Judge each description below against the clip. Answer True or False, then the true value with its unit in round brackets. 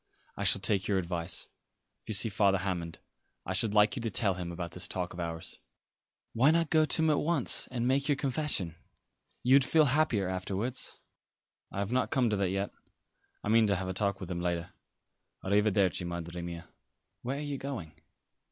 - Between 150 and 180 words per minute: False (200 wpm)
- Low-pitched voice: True (100 Hz)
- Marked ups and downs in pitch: True (6.0 semitones)